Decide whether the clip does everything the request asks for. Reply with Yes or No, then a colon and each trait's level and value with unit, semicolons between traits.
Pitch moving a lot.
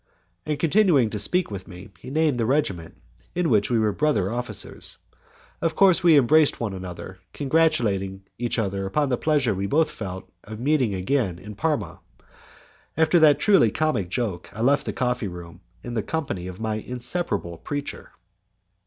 Yes: wide, 7.6 semitones